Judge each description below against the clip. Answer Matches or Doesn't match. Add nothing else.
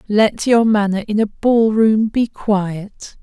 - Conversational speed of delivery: Matches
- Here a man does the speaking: Doesn't match